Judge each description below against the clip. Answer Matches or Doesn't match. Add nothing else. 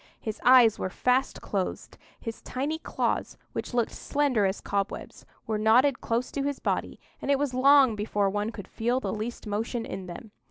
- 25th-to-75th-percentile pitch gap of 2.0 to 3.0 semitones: Doesn't match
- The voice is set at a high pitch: Matches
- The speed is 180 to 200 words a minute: Matches